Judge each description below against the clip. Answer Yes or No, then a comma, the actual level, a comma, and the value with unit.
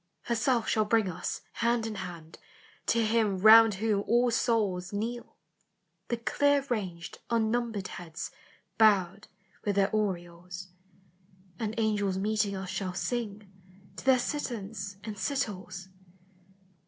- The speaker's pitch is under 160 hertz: No, high, 210 Hz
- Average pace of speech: No, slow, 120 wpm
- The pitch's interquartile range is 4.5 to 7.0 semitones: No, average, 3.3 semitones